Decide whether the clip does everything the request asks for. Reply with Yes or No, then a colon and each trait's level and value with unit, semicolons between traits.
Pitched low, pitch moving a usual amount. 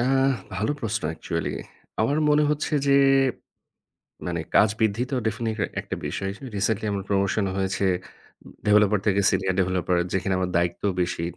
Yes: low, 100 Hz; average, 3.0 semitones